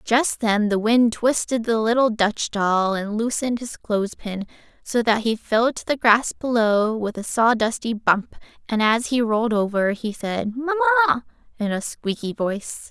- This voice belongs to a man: No, female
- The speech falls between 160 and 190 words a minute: Yes, average, 175 wpm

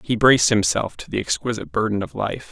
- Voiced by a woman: No, male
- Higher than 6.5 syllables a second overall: No, 6.2 syllables/s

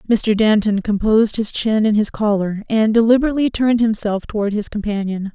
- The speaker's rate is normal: Yes, average, 170 wpm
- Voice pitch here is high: Yes, high, 215 Hz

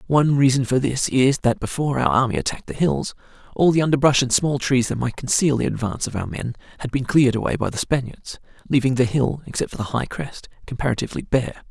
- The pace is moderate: No, fast, 220 wpm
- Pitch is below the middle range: Yes, low, 130 Hz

